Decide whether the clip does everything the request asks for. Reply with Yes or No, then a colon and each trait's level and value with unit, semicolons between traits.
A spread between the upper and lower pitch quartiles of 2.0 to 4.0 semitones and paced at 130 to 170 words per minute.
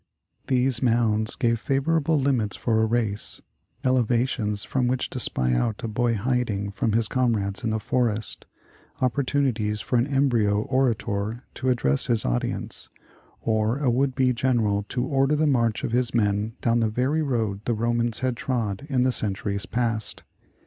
Yes: average, 3.1 semitones; average, 165 wpm